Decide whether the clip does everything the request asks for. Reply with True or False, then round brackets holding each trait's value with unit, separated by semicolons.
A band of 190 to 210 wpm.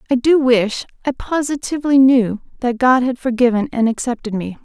False (170 wpm)